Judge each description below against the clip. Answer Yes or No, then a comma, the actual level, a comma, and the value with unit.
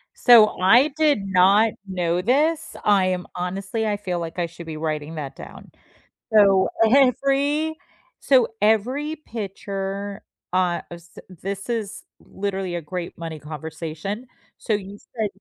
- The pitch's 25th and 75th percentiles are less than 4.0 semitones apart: No, average, 4.4 semitones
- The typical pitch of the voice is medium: No, high, 195 Hz